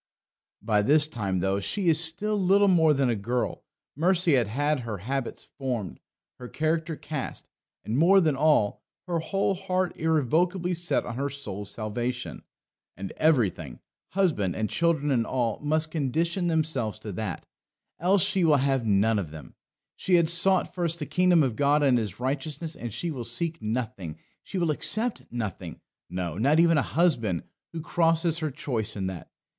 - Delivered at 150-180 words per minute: Yes, average, 170 wpm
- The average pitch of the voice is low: No, medium, 145 Hz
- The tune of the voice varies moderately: No, wide, 6.9 semitones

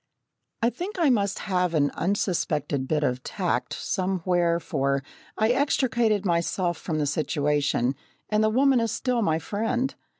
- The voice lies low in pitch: No, medium, 185 Hz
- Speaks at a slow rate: No, average, 145 wpm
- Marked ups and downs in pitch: Yes, wide, 6.5 semitones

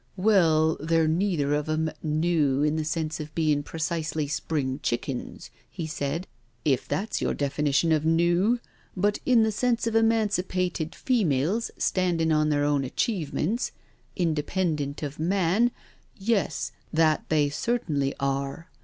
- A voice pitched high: No, medium, 160 Hz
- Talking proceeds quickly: No, average, 145 wpm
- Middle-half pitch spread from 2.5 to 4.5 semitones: Yes, average, 4.0 semitones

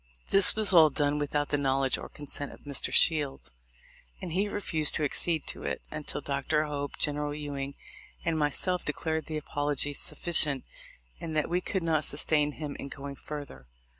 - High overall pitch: No, medium, 150 Hz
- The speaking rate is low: No, average, 175 wpm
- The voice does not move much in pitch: Yes, narrow, 1.9 semitones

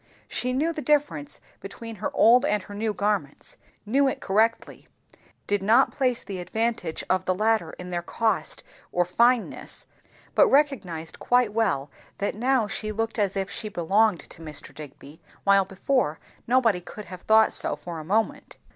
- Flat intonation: No, average, 4.7 semitones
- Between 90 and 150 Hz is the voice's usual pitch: No, high, 210 Hz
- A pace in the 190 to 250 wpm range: No, average, 165 wpm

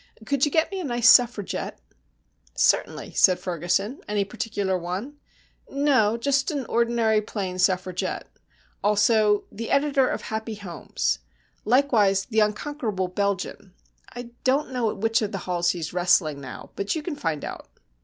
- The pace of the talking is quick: No, average, 150 wpm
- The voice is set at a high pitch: Yes, high, 215 Hz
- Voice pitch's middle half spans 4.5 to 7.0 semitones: Yes, average, 5.0 semitones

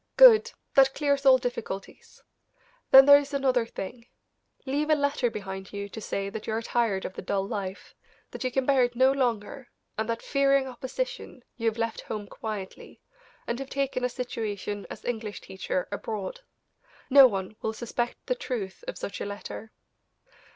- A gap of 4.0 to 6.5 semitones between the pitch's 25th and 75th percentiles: Yes, average, 4.7 semitones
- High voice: Yes, high, 240 Hz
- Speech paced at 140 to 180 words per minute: Yes, average, 175 wpm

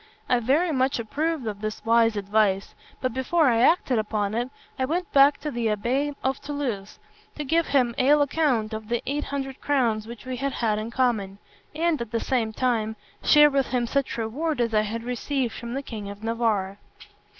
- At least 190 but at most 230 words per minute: Yes, average, 195 wpm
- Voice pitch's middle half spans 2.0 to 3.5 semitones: No, average, 4.2 semitones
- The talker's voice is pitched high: Yes, high, 245 Hz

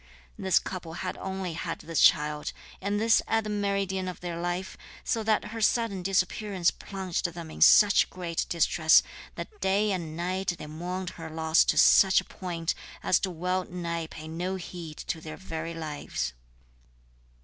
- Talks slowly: No, average, 170 wpm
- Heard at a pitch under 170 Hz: No, medium, 180 Hz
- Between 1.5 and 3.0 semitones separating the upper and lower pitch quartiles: Yes, narrow, 2.6 semitones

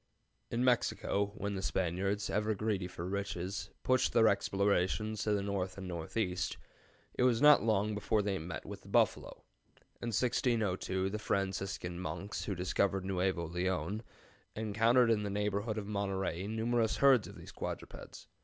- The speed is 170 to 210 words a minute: No, average, 155 wpm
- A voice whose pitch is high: No, low, 100 Hz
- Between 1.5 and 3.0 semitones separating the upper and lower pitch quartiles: Yes, narrow, 2.6 semitones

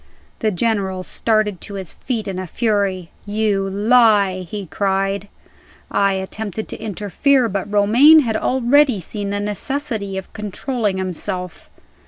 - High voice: Yes, high, 205 Hz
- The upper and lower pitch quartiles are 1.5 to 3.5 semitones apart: Yes, narrow, 2.6 semitones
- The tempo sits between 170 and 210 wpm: No, slow, 135 wpm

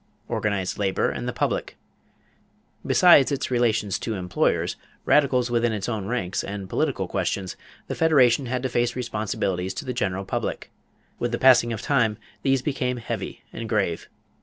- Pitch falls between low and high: No, low, 120 Hz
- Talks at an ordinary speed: Yes, average, 160 wpm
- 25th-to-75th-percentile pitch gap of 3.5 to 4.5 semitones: Yes, average, 4.0 semitones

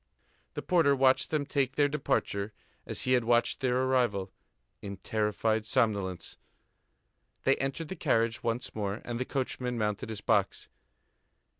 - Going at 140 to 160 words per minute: Yes, average, 145 wpm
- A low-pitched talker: Yes, low, 120 Hz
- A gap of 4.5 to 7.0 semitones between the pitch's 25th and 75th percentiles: No, average, 4.0 semitones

